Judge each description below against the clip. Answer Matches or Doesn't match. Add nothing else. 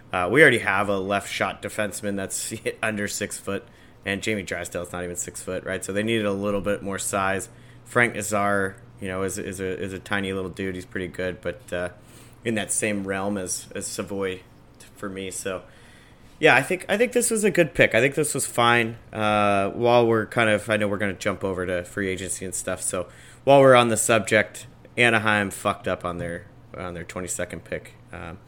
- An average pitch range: Matches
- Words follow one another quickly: Matches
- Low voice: Matches